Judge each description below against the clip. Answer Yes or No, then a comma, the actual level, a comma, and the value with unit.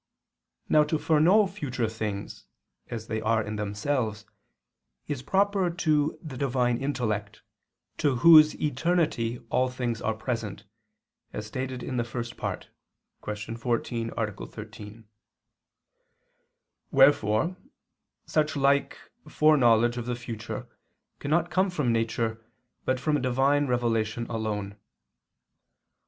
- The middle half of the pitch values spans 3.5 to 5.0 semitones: Yes, average, 4.7 semitones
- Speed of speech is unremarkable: No, slow, 115 wpm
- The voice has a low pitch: Yes, low, 120 Hz